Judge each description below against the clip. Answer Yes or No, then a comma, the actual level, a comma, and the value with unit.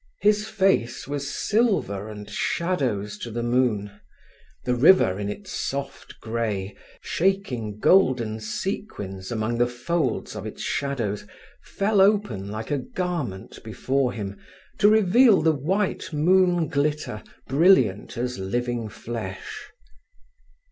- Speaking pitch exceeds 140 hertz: No, low, 125 Hz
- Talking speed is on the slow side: Yes, slow, 120 wpm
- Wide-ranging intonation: Yes, wide, 8.9 semitones